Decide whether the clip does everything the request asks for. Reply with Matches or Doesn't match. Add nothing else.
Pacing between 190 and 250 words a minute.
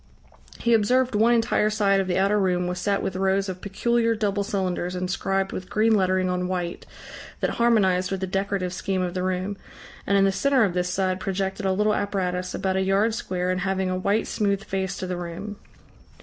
Matches